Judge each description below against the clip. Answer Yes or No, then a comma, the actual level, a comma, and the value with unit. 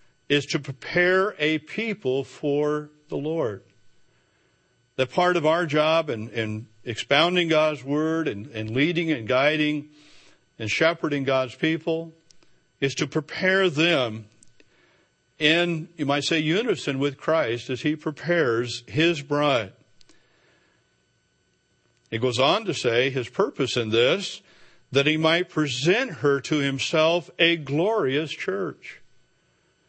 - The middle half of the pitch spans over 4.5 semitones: No, average, 4.0 semitones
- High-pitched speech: No, medium, 150 Hz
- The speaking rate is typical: No, slow, 120 wpm